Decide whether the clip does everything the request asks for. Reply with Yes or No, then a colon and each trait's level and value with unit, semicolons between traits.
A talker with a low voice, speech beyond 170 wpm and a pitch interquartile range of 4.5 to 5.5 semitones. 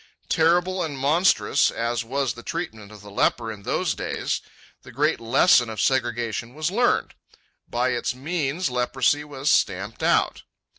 No: low, 130 Hz; average, 150 wpm; average, 5.2 semitones